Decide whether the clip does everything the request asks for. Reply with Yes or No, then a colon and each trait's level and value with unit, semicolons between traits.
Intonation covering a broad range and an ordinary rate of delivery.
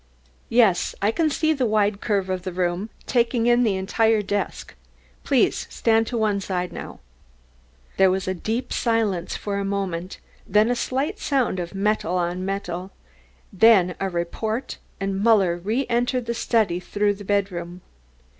No: average, 3.6 semitones; average, 160 wpm